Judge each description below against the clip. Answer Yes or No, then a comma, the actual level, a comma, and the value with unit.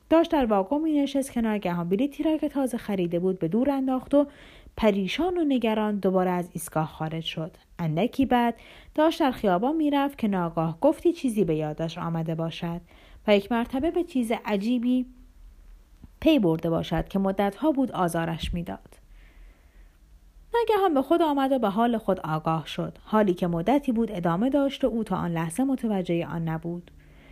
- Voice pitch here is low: No, high, 205 Hz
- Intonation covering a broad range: Yes, wide, 8.2 semitones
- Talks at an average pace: No, fast, 170 wpm